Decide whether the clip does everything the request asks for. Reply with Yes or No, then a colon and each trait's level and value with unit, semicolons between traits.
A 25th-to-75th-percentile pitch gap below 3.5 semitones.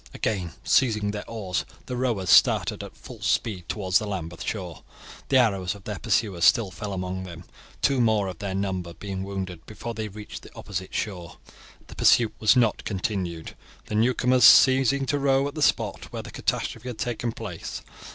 No: average, 4.0 semitones